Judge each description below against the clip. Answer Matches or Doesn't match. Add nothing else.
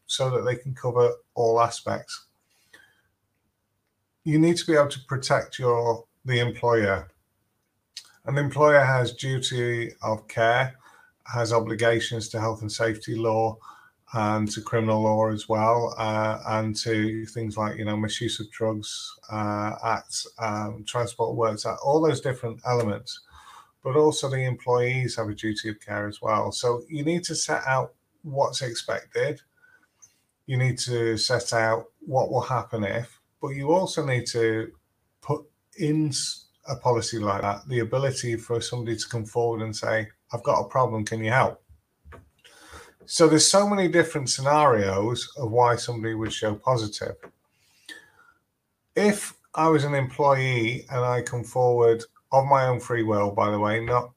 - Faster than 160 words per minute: Doesn't match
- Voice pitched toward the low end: Matches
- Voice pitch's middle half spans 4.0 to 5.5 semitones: Doesn't match